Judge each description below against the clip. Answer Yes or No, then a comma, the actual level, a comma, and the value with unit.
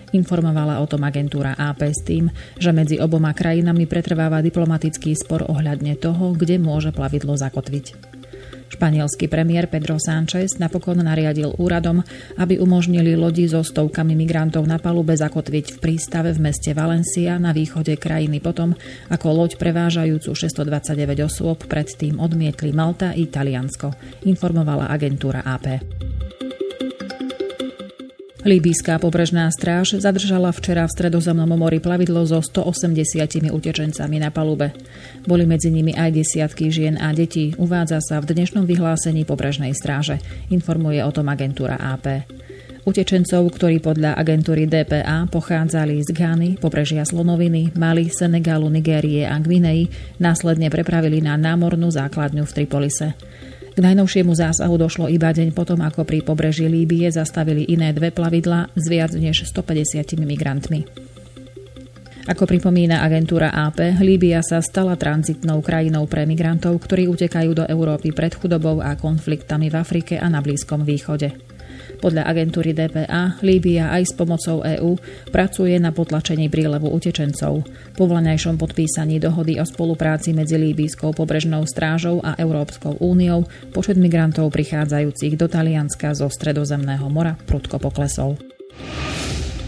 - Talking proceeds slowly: No, average, 130 wpm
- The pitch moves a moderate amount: No, narrow, 2.0 semitones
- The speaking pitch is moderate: Yes, medium, 160 Hz